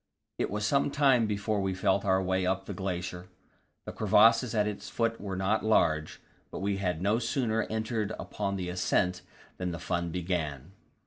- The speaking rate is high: No, average, 185 wpm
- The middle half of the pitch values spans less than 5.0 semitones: Yes, average, 3.2 semitones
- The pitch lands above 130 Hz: No, low, 100 Hz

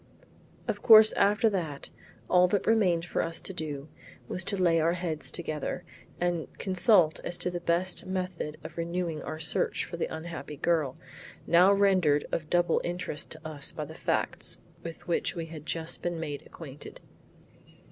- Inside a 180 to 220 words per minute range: No, average, 165 wpm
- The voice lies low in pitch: No, medium, 170 Hz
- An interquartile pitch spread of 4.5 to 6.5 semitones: No, narrow, 2.4 semitones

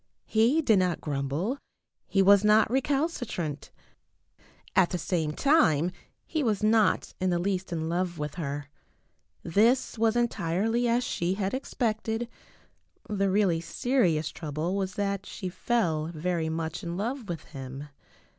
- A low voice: No, high, 190 Hz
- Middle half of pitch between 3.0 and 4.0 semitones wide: No, wide, 5.4 semitones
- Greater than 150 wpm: No, average, 140 wpm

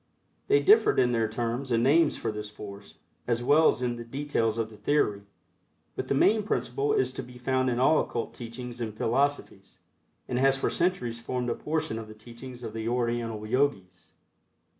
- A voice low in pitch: Yes, low, 120 Hz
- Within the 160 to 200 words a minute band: Yes, average, 190 wpm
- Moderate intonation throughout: Yes, average, 3.4 semitones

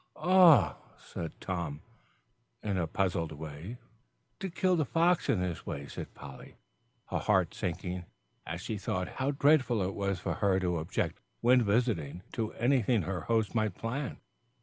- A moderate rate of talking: Yes, average, 155 wpm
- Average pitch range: No, wide, 6.4 semitones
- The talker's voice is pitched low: Yes, low, 100 Hz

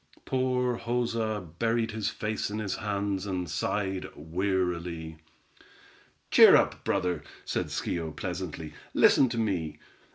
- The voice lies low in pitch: Yes, low, 100 Hz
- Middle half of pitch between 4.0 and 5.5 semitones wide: Yes, average, 4.3 semitones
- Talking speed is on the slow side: Yes, slow, 120 wpm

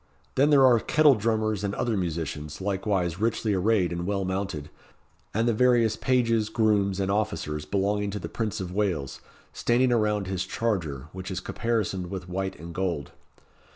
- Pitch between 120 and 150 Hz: No, low, 100 Hz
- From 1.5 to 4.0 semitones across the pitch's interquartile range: Yes, average, 3.5 semitones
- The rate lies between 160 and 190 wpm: Yes, average, 165 wpm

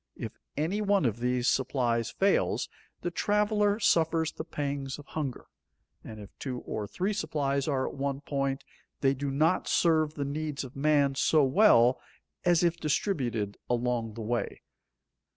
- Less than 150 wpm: No, average, 155 wpm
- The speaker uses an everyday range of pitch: Yes, average, 4.4 semitones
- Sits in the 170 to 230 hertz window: No, medium, 140 Hz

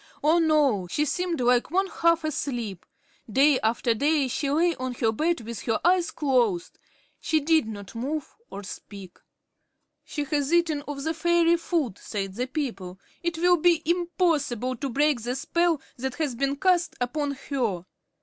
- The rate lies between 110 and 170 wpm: Yes, average, 165 wpm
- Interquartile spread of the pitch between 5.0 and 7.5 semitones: Yes, wide, 5.5 semitones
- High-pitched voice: Yes, very high, 285 Hz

